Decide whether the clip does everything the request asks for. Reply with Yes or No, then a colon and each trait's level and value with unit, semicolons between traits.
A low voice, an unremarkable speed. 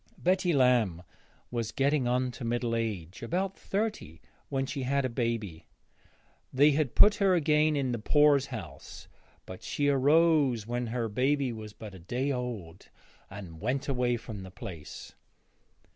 Yes: low, 125 Hz; average, 150 wpm